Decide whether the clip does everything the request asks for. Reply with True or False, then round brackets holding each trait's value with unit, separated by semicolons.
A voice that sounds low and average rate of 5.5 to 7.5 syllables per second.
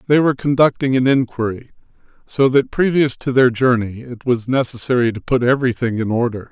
True (125 Hz; 5.7 syllables/s)